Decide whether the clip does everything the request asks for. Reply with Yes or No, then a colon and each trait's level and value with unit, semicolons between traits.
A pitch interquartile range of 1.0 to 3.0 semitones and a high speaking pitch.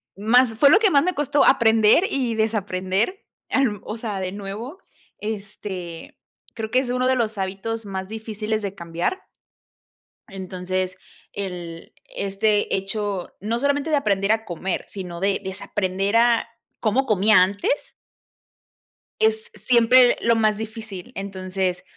No: average, 3.4 semitones; high, 210 Hz